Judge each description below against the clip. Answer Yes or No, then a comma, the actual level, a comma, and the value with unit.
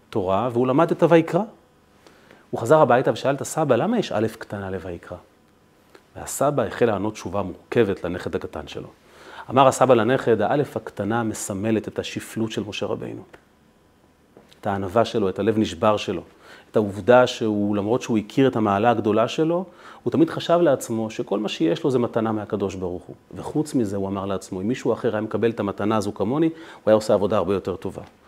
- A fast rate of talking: Yes, fast, 185 wpm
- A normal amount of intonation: Yes, average, 3.6 semitones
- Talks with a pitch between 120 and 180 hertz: No, low, 110 Hz